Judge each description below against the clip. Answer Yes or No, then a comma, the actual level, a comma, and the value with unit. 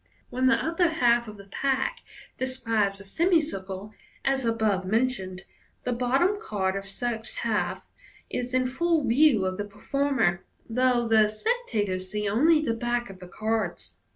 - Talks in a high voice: Yes, high, 235 Hz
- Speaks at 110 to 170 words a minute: Yes, average, 155 wpm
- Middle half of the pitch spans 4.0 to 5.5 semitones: Yes, average, 4.7 semitones